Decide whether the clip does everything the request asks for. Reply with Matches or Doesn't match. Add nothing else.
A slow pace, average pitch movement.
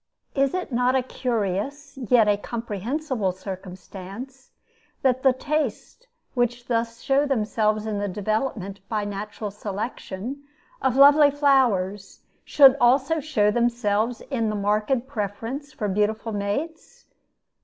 Matches